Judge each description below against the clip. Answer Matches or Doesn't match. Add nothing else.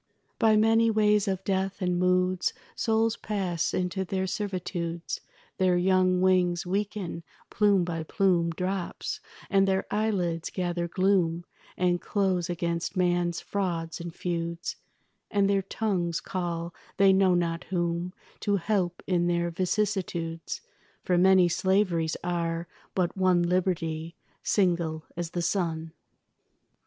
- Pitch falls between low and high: Matches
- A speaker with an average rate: Doesn't match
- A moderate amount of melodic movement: Doesn't match